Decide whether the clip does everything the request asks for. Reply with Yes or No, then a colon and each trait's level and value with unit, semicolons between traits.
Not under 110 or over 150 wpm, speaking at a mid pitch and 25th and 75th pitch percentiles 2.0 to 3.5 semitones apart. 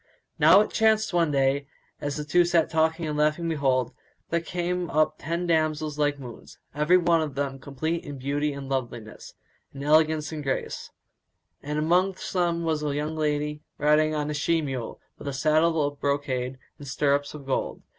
No: average, 180 wpm; medium, 150 Hz; narrow, 2.6 semitones